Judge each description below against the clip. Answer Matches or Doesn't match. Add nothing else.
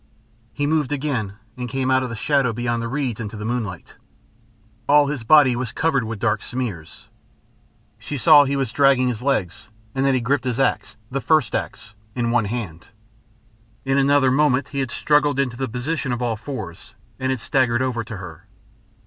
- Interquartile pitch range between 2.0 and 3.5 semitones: Matches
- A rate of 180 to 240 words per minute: Matches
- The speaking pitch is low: Matches